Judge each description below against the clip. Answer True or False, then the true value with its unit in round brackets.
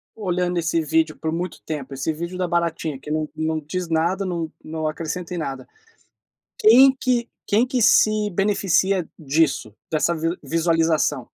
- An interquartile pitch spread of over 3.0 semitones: False (2.7 semitones)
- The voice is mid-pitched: True (165 Hz)